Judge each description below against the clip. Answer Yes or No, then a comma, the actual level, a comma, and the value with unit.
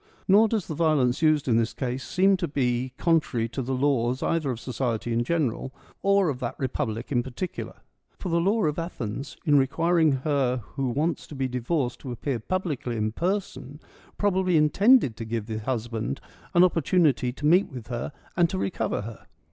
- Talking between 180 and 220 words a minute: Yes, average, 185 wpm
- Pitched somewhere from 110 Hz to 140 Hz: Yes, low, 135 Hz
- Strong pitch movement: Yes, wide, 5.7 semitones